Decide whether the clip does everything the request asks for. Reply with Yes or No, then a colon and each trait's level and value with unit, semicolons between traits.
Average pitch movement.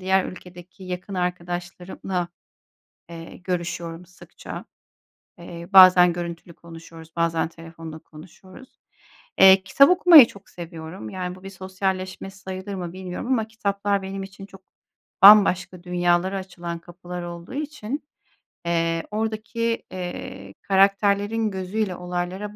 No: narrow, 2.3 semitones